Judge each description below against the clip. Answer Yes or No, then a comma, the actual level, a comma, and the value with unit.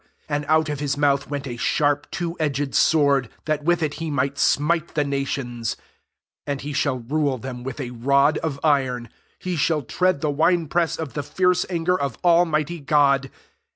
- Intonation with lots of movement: No, narrow, 2.5 semitones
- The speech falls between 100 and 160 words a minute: No, average, 190 wpm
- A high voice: No, medium, 145 Hz